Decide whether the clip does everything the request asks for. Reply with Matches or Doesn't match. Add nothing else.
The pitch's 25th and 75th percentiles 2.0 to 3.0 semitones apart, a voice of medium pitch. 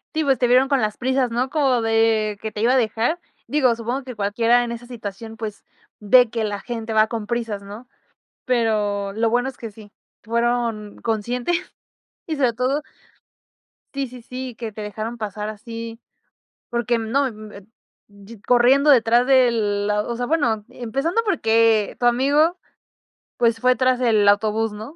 Doesn't match